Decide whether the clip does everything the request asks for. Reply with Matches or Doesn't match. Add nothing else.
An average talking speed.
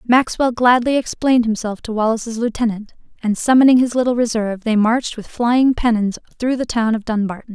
Matches